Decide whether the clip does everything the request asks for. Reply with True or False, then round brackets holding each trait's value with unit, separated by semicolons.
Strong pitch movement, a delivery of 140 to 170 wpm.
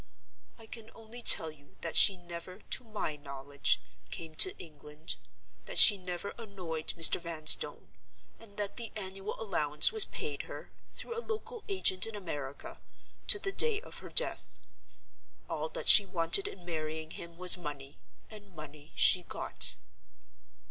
True (6.2 semitones; 155 wpm)